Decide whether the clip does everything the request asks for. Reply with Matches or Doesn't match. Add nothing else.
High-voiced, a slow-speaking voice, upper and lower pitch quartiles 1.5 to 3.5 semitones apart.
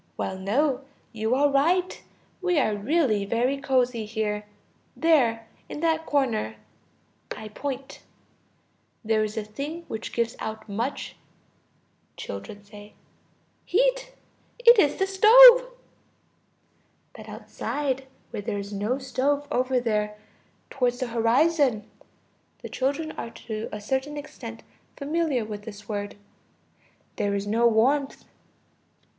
Doesn't match